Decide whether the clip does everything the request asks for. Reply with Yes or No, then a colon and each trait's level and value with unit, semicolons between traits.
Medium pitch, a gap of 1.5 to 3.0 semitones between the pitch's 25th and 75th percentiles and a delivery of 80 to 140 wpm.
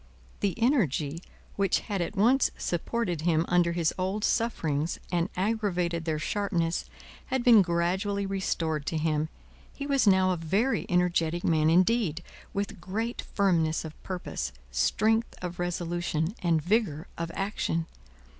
No: medium, 175 Hz; average, 3.7 semitones; slow, 135 wpm